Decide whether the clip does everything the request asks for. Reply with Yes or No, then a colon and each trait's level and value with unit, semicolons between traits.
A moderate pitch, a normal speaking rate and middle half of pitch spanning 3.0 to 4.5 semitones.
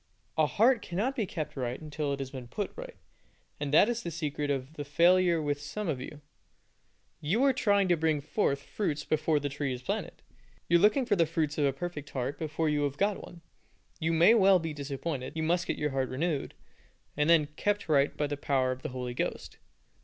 No: medium, 155 Hz; fast, 220 wpm; average, 3.8 semitones